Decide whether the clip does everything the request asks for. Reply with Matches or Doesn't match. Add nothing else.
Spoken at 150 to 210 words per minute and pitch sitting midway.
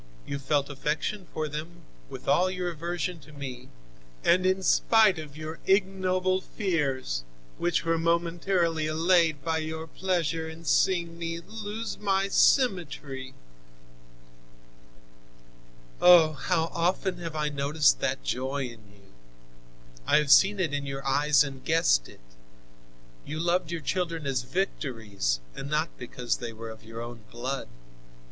Doesn't match